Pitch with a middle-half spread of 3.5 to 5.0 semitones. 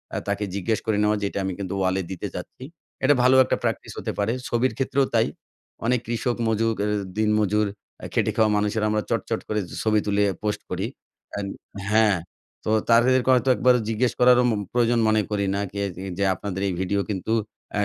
No: average, 2.7 semitones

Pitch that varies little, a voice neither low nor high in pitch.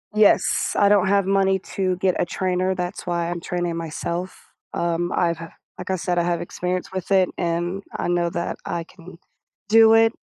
Yes: narrow, 1.8 semitones; medium, 180 Hz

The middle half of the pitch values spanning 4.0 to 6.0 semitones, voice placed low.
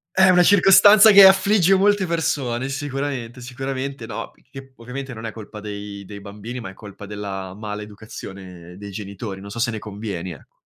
Yes: wide, 5.5 semitones; low, 115 Hz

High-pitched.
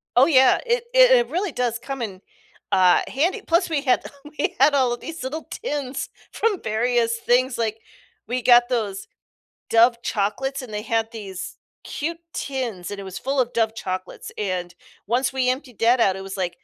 Yes: high, 245 Hz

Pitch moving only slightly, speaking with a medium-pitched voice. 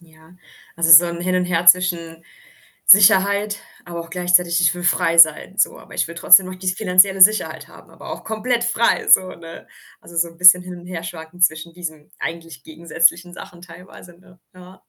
Yes: narrow, 1.7 semitones; medium, 175 Hz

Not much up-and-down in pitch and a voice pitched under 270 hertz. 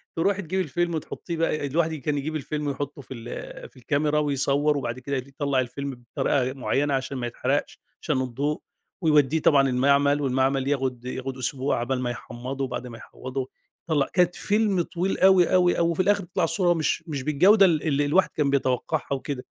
No: average, 3.5 semitones; medium, 140 Hz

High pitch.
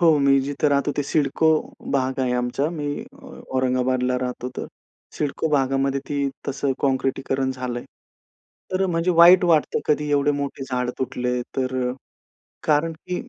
No: low, 135 Hz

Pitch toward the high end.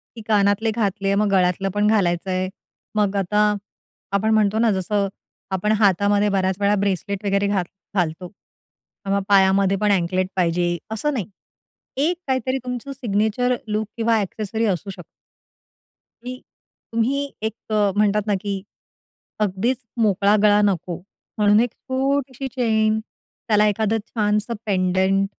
Yes: high, 205 Hz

